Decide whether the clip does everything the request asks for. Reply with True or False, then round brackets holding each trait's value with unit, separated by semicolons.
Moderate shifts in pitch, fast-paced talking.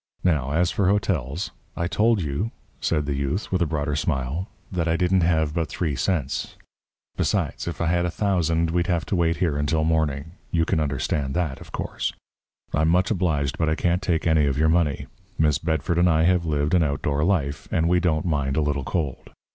True (3.2 semitones; 210 wpm)